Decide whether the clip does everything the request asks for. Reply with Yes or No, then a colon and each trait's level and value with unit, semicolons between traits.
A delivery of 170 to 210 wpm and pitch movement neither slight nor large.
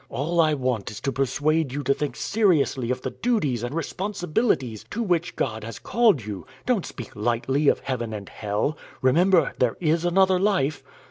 No: average, 180 wpm; wide, 6.5 semitones